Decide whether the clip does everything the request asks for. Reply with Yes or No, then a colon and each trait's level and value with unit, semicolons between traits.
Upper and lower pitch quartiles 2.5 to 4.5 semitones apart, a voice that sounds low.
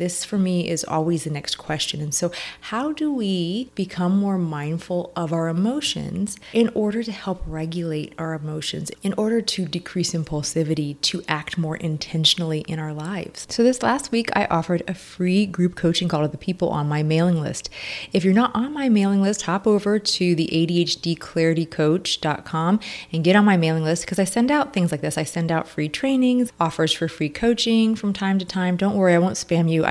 No: average, 3.8 semitones; medium, 175 Hz